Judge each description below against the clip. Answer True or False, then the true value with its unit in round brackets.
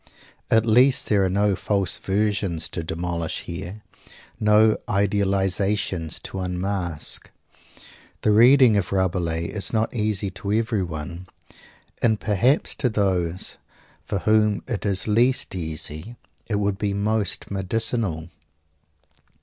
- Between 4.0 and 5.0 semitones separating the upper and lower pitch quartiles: False (3.1 semitones)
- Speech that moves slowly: True (115 wpm)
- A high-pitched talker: False (100 Hz)